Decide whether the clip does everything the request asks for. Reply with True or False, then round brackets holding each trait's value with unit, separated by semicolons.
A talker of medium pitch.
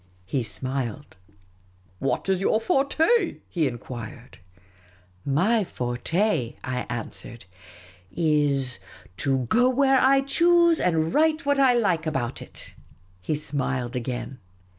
True (150 Hz)